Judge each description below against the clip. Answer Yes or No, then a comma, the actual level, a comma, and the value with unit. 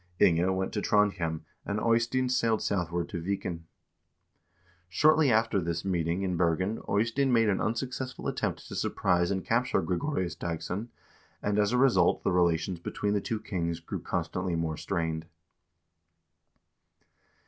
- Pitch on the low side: Yes, very low, 95 Hz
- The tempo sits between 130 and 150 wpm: Yes, average, 140 wpm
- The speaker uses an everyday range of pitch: Yes, average, 4.9 semitones